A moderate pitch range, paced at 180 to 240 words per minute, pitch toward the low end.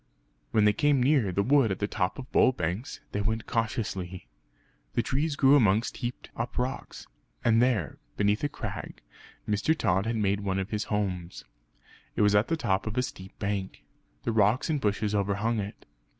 Yes: average, 3.8 semitones; average, 185 wpm; low, 105 Hz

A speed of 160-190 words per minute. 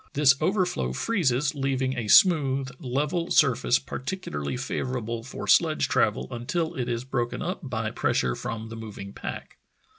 No: average, 150 wpm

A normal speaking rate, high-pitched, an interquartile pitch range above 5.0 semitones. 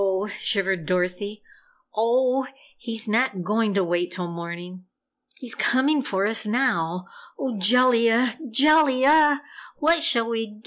No: slow, 125 wpm; high, 225 Hz; wide, 5.4 semitones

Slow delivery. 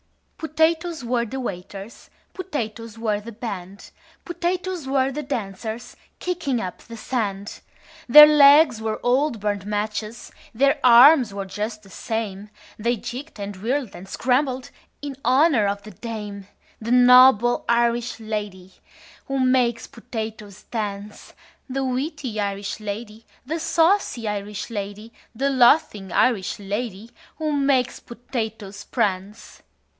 Yes: slow, 125 wpm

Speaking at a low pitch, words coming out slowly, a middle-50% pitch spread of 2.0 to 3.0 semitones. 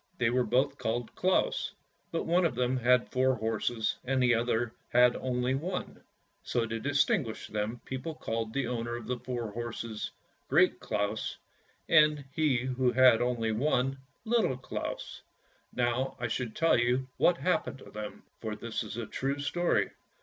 No: low, 125 Hz; average, 170 wpm; average, 2.7 semitones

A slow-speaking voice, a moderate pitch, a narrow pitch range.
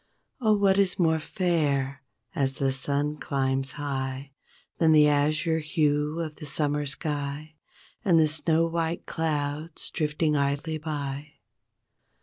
Yes: slow, 130 wpm; medium, 150 Hz; narrow, 2.2 semitones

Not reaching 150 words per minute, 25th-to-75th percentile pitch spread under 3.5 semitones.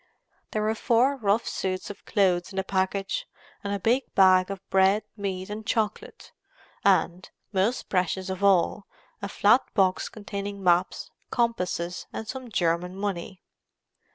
Yes: average, 140 wpm; narrow, 2.5 semitones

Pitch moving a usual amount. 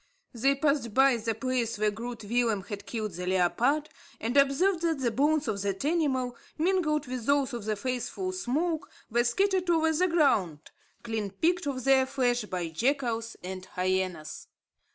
No: wide, 5.7 semitones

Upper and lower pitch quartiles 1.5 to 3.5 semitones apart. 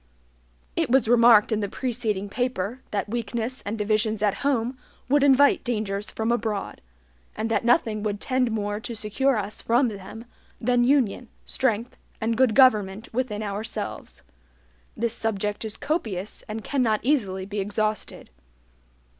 Yes: average, 2.9 semitones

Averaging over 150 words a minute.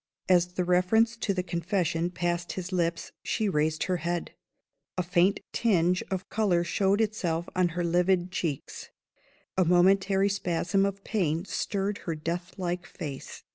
No: average, 145 wpm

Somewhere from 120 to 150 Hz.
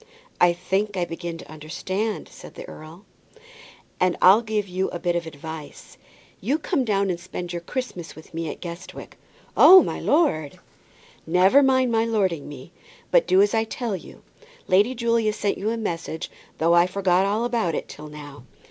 No: medium, 185 Hz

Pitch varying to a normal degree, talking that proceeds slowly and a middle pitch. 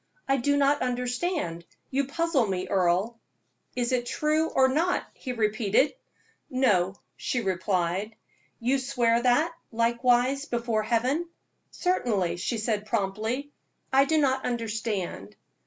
No: average, 4.3 semitones; slow, 125 wpm; high, 240 Hz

